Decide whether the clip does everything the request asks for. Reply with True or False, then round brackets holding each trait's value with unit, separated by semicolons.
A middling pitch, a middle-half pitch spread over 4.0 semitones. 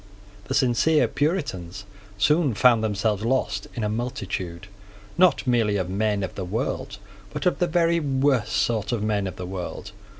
False (110 Hz; 5.1 semitones)